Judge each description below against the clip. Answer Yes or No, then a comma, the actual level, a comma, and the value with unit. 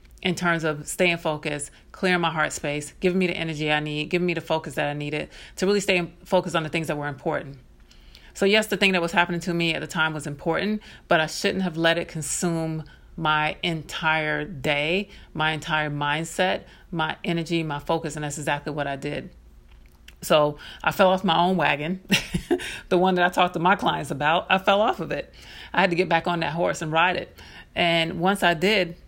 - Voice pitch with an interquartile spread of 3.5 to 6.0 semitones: No, average, 2.9 semitones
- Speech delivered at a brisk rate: Yes, fast, 215 wpm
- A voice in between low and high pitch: Yes, medium, 165 Hz